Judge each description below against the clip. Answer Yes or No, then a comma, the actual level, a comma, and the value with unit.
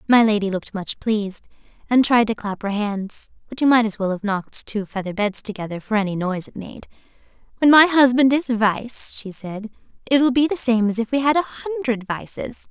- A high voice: Yes, high, 230 Hz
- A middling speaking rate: No, fast, 215 wpm